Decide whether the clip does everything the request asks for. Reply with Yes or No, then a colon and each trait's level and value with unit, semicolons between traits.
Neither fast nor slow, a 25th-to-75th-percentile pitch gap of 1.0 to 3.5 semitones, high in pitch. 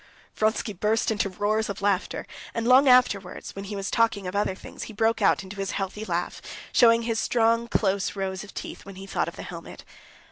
No: fast, 210 wpm; narrow, 2.6 semitones; high, 210 Hz